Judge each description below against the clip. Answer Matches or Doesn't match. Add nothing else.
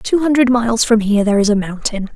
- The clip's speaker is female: Matches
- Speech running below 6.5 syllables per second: Doesn't match